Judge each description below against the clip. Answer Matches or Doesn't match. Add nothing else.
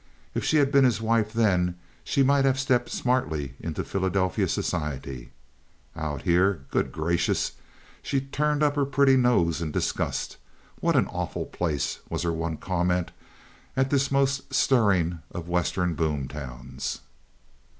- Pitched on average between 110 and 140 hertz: Doesn't match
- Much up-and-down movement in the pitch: Matches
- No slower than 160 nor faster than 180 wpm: Doesn't match